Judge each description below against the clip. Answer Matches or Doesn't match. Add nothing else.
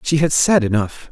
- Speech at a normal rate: Doesn't match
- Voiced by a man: Matches